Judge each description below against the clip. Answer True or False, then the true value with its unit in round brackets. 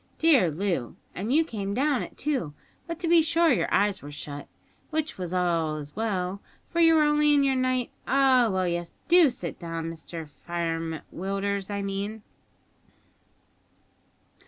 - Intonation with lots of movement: True (8.5 semitones)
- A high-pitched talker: True (200 Hz)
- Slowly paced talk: False (160 wpm)